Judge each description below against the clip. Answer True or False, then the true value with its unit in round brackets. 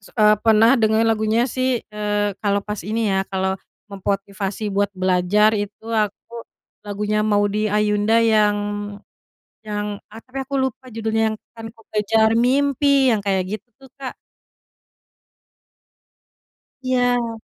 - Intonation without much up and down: True (1.8 semitones)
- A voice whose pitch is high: True (215 Hz)